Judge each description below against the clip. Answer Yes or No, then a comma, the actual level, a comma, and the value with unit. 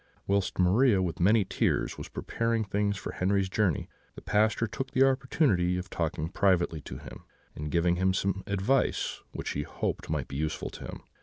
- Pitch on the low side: Yes, very low, 95 Hz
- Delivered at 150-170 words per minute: No, average, 180 wpm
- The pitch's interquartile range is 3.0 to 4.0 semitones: Yes, average, 3.6 semitones